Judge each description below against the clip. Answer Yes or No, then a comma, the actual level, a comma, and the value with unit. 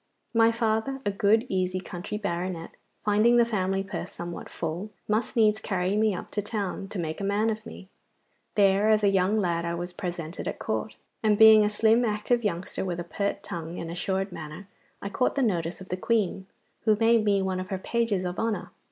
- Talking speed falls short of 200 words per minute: No, fast, 205 wpm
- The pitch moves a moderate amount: Yes, average, 3.0 semitones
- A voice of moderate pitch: No, high, 200 Hz